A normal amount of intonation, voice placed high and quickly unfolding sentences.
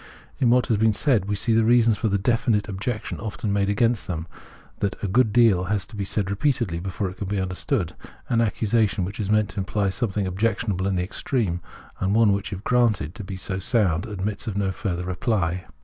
No: average, 3.0 semitones; low, 100 Hz; fast, 220 wpm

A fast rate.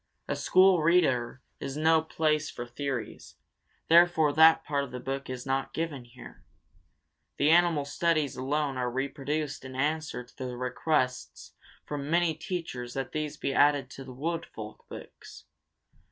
No: average, 155 wpm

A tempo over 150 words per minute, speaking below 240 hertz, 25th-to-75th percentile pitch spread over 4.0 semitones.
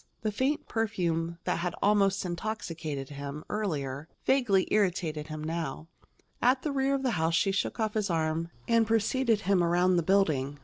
Yes: average, 170 wpm; medium, 185 Hz; average, 5.2 semitones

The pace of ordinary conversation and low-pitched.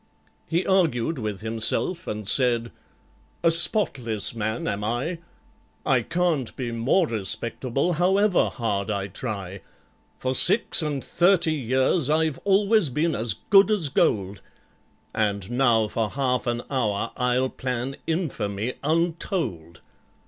No: slow, 125 wpm; low, 130 Hz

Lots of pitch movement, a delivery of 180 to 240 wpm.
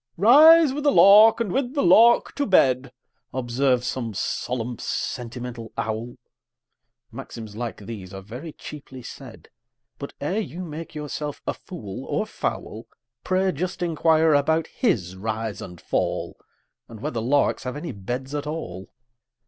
No: wide, 7.4 semitones; average, 145 wpm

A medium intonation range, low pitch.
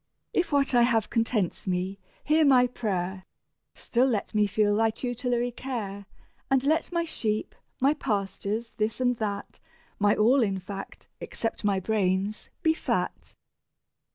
No: average, 3.8 semitones; high, 220 Hz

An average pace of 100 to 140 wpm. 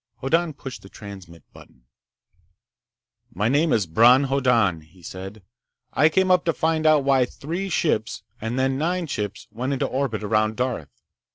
No: average, 160 wpm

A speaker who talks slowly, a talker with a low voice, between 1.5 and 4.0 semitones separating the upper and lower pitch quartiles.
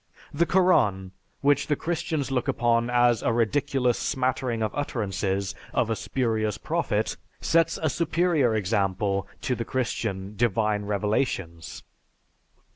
No: slow, 120 wpm; low, 115 Hz; average, 4.9 semitones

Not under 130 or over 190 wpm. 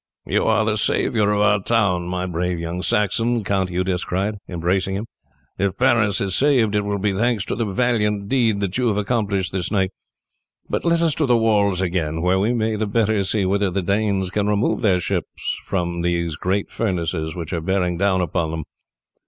No: average, 200 wpm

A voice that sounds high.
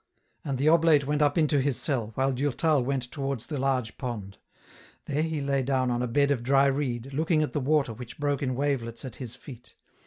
No: low, 135 Hz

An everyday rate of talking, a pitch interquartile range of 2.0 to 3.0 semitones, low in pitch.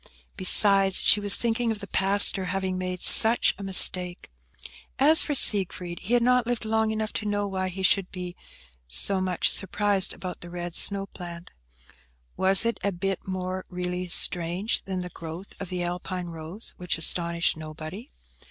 No: average, 170 wpm; narrow, 2.4 semitones; medium, 185 Hz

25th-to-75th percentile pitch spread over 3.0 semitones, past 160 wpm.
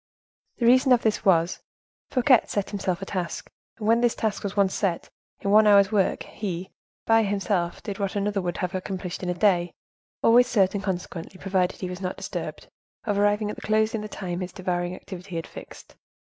No: average, 2.7 semitones; average, 200 wpm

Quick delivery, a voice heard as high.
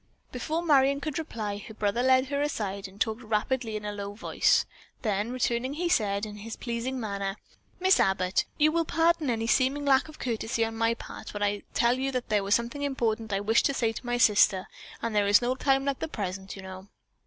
Yes: fast, 225 wpm; high, 230 Hz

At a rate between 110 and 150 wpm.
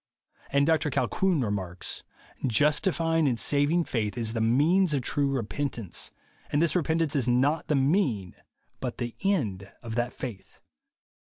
Yes: average, 145 wpm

